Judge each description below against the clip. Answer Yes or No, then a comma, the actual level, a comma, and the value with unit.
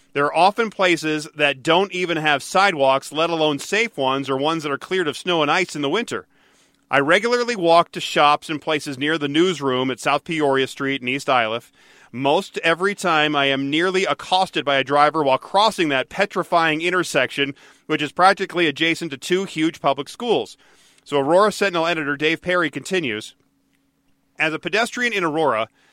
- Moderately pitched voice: Yes, medium, 160 Hz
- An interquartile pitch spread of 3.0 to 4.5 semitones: Yes, average, 4.0 semitones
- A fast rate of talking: No, average, 180 wpm